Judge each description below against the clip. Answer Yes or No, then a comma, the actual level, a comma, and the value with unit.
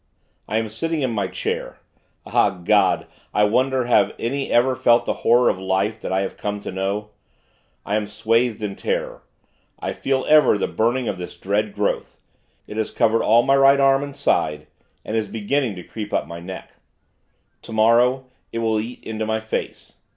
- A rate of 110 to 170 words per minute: No, average, 185 wpm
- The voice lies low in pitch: Yes, low, 110 Hz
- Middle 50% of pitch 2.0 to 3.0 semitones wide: No, average, 3.4 semitones